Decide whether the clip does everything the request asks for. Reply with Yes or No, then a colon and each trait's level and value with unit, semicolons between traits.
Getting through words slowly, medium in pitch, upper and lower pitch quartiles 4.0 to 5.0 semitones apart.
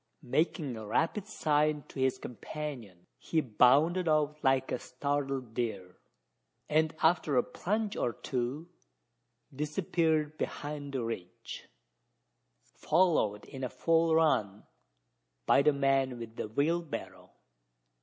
Yes: slow, 115 wpm; medium, 145 Hz; average, 4.3 semitones